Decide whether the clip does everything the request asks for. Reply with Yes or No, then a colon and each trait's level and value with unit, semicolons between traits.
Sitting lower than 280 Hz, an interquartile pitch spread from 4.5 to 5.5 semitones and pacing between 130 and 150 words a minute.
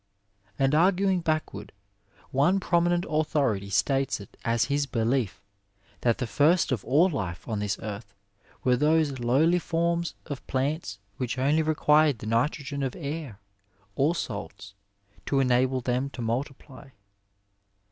Yes: low, 135 Hz; average, 4.9 semitones; slow, 135 wpm